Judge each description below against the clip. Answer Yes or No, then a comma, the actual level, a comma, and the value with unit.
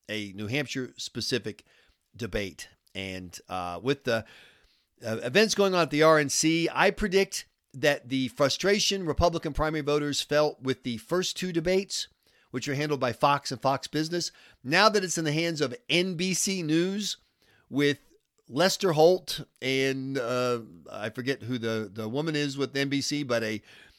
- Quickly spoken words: No, average, 160 wpm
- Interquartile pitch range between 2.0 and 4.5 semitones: No, average, 5.1 semitones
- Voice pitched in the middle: Yes, medium, 145 Hz